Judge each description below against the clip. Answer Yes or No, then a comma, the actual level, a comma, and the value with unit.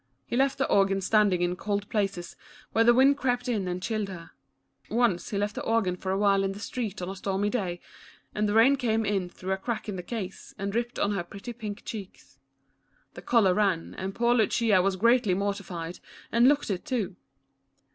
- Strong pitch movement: No, average, 3.4 semitones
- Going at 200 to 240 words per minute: Yes, fast, 205 wpm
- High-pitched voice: Yes, high, 205 Hz